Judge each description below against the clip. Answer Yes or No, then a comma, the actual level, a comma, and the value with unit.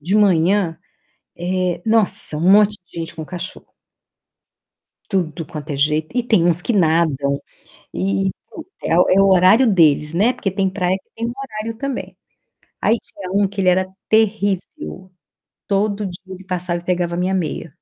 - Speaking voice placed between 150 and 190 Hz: Yes, medium, 185 Hz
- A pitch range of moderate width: Yes, average, 3.6 semitones